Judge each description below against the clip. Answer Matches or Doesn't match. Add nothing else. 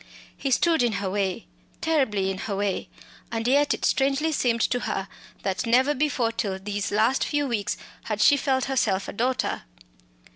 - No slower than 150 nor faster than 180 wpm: Matches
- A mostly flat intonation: Doesn't match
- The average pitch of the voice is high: Matches